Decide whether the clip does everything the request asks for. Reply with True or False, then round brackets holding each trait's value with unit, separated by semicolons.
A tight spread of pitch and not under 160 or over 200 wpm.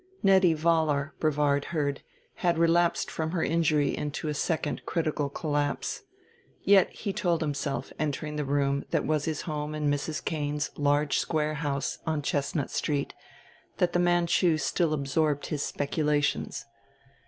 False (2.2 semitones; 140 wpm)